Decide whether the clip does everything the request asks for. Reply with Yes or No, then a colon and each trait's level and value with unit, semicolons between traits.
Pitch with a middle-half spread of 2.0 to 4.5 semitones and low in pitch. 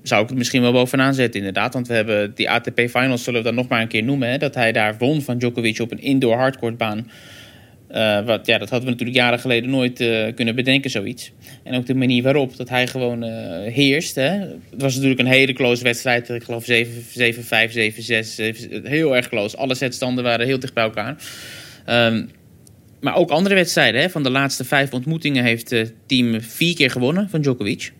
Yes: narrow, 2.5 semitones; low, 125 Hz